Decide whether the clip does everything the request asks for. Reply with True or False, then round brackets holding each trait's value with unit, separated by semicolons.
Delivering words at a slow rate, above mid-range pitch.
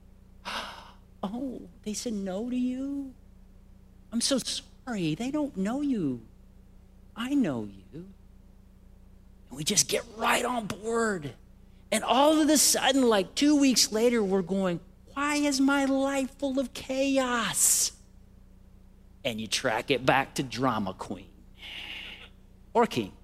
True (130 wpm; 205 Hz)